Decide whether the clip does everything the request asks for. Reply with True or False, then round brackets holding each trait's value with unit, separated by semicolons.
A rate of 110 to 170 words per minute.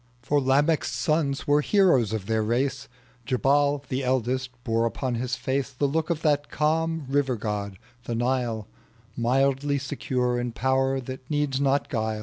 True (155 wpm)